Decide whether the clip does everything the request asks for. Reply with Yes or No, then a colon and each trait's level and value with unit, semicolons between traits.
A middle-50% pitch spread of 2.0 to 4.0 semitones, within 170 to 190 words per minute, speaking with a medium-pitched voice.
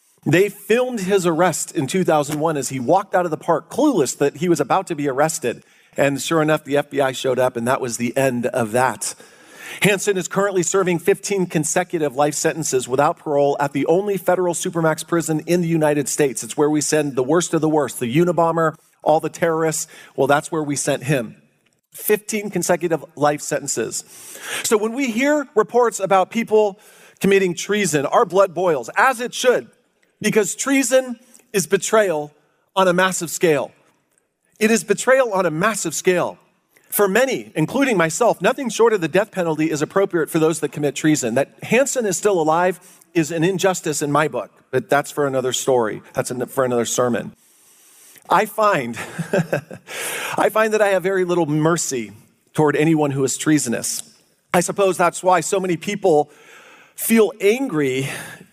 No: average, 5.1 semitones; average, 175 wpm; medium, 170 Hz